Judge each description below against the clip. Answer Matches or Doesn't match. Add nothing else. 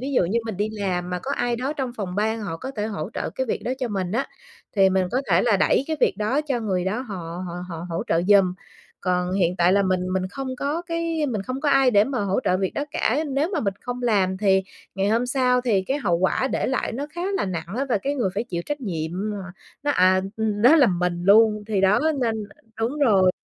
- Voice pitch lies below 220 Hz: Matches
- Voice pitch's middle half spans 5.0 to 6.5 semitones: Matches